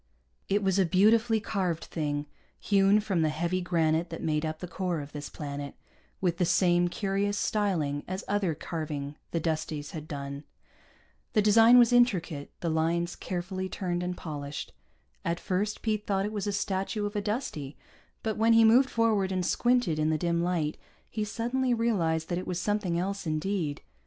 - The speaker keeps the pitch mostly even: No, average, 4.5 semitones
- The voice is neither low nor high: Yes, medium, 180 Hz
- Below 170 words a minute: No, average, 180 wpm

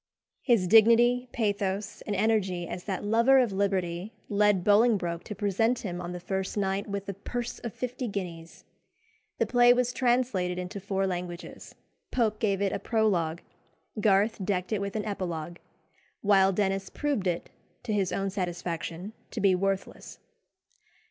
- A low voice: No, high, 200 Hz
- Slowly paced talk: No, average, 155 wpm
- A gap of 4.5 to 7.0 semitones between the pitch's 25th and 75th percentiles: No, average, 3.2 semitones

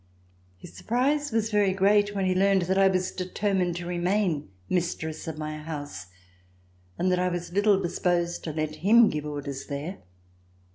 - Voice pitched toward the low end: No, medium, 180 Hz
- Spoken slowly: No, average, 165 wpm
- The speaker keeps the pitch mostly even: No, average, 3.9 semitones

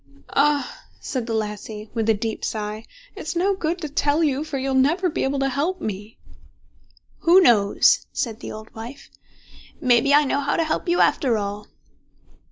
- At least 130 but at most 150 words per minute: No, average, 180 wpm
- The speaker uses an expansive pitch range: Yes, wide, 5.7 semitones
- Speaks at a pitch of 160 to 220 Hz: No, very high, 270 Hz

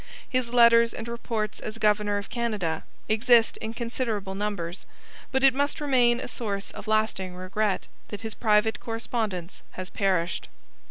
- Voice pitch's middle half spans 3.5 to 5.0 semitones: No, average, 2.9 semitones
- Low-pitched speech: No, high, 220 Hz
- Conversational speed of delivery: Yes, average, 150 wpm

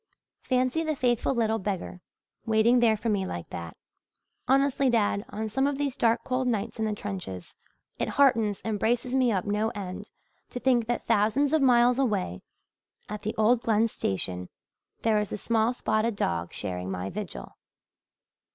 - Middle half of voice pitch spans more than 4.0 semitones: No, average, 3.4 semitones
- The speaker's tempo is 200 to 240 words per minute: No, average, 170 wpm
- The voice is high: Yes, high, 220 Hz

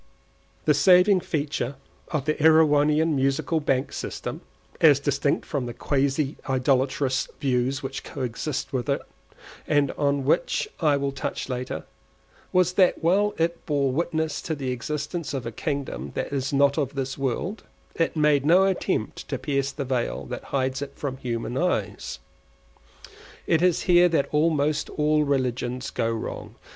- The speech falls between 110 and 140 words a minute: No, average, 150 wpm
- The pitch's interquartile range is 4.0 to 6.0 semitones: No, average, 2.9 semitones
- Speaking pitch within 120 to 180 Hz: Yes, medium, 140 Hz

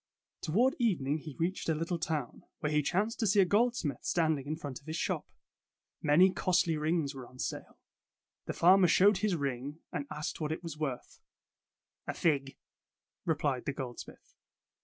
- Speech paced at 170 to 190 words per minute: Yes, average, 175 wpm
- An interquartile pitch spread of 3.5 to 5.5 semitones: Yes, average, 4.1 semitones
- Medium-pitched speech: Yes, medium, 160 Hz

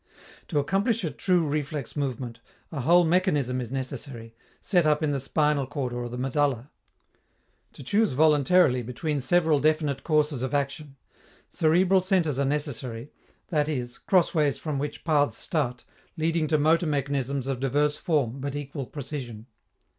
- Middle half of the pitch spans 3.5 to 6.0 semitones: No, average, 3.1 semitones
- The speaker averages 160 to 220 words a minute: No, average, 150 wpm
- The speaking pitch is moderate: Yes, medium, 145 Hz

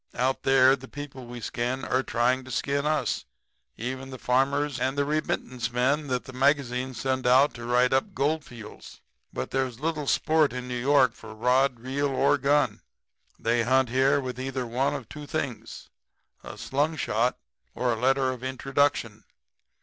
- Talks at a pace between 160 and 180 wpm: Yes, average, 170 wpm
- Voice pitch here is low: Yes, low, 130 Hz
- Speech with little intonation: Yes, narrow, 2.2 semitones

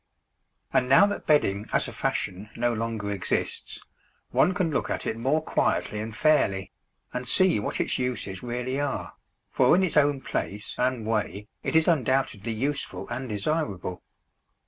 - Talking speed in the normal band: Yes, average, 160 wpm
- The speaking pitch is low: Yes, low, 125 Hz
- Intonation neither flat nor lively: No, wide, 5.7 semitones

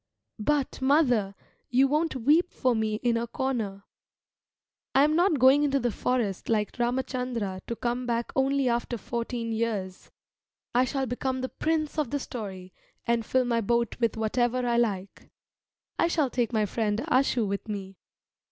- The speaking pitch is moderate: No, high, 240 Hz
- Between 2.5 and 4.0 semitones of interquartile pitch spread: Yes, average, 3.1 semitones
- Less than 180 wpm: Yes, average, 160 wpm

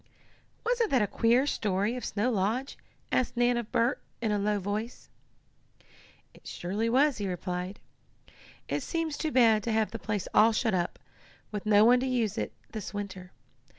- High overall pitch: Yes, high, 220 Hz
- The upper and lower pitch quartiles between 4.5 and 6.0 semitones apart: No, average, 3.4 semitones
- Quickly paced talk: No, average, 175 wpm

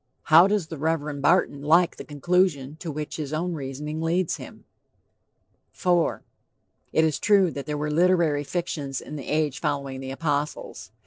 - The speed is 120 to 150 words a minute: No, average, 165 wpm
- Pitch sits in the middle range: Yes, medium, 155 Hz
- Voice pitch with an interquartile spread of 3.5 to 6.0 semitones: No, average, 3.0 semitones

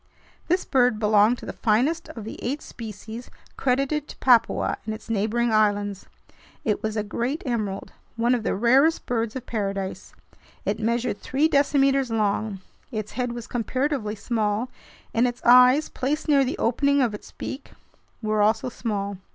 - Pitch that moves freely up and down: No, average, 3.4 semitones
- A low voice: No, high, 235 Hz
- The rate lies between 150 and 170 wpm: Yes, average, 160 wpm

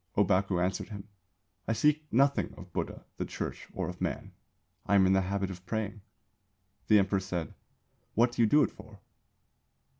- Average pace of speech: Yes, average, 175 wpm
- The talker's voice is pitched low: Yes, low, 100 Hz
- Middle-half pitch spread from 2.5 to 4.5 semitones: Yes, average, 2.9 semitones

